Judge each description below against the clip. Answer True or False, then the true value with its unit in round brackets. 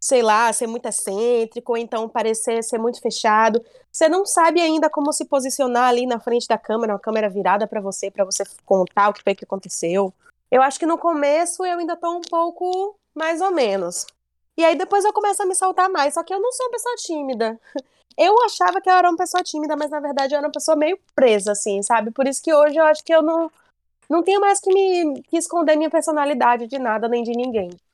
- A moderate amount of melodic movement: False (7.0 semitones)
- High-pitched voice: True (290 Hz)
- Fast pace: True (230 wpm)